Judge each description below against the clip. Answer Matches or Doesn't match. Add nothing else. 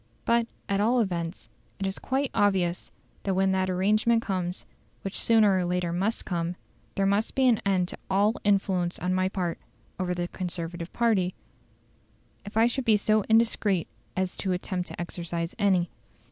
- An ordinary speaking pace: Matches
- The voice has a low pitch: Doesn't match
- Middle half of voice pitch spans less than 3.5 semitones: Matches